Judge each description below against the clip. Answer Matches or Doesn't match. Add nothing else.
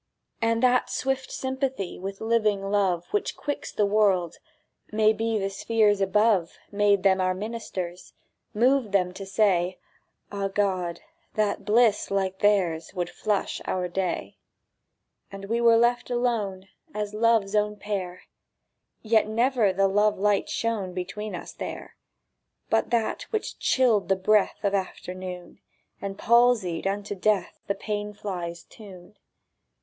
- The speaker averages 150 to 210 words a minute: Doesn't match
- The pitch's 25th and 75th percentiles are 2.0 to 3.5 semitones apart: Matches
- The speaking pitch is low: Doesn't match